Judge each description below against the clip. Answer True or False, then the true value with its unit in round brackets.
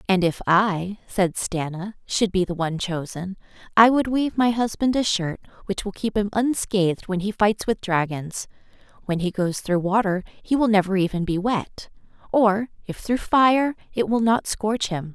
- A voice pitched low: False (200 Hz)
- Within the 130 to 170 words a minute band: False (185 wpm)